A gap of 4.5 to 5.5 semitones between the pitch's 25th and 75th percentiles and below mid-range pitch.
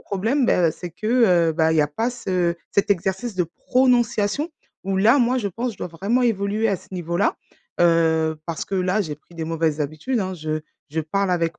No: average, 5.2 semitones; medium, 185 Hz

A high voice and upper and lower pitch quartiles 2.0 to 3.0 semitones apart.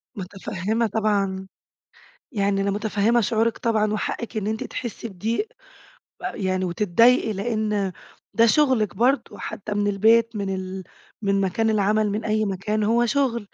Yes: high, 215 Hz; narrow, 2.5 semitones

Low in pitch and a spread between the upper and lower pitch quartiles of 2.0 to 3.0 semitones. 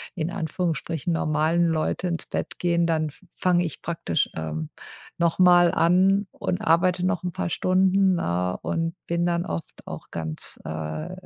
No: medium, 170 Hz; narrow, 2.6 semitones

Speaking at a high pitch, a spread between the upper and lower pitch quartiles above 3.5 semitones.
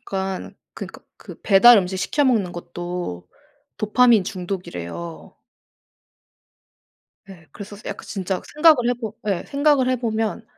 Yes: high, 200 Hz; average, 5.1 semitones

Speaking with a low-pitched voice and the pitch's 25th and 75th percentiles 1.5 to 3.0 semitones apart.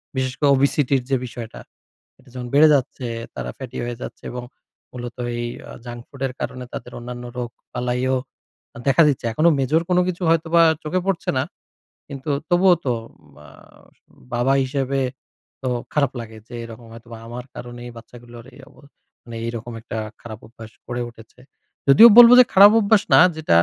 No: low, 125 Hz; average, 3.4 semitones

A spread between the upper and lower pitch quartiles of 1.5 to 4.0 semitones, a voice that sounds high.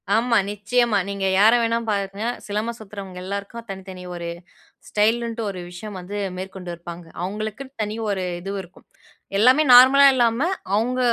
Yes: average, 3.3 semitones; high, 210 Hz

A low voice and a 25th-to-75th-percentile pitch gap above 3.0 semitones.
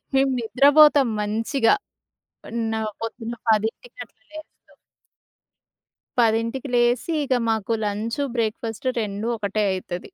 No: high, 230 Hz; average, 3.5 semitones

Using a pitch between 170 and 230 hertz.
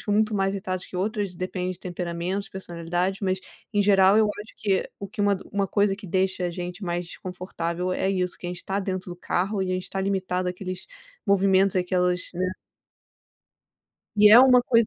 Yes: high, 190 Hz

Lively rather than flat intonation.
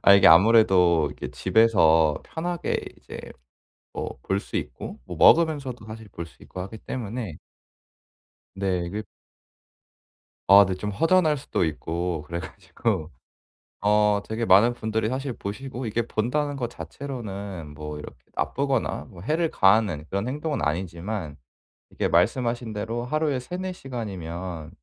Yes: wide, 6.0 semitones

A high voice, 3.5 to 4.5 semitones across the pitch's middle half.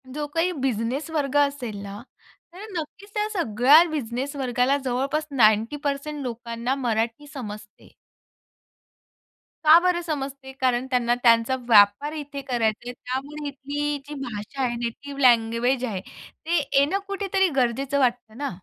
Yes: very high, 265 Hz; average, 3.8 semitones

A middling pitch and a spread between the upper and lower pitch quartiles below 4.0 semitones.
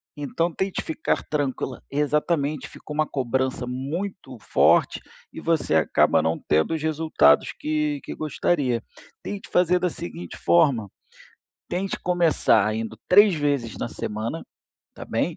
No: medium, 150 Hz; average, 5.1 semitones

